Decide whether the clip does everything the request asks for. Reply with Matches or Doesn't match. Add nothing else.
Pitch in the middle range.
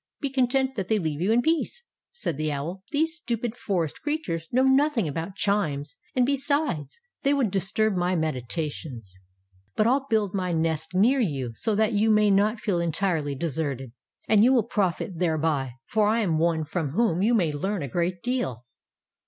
Doesn't match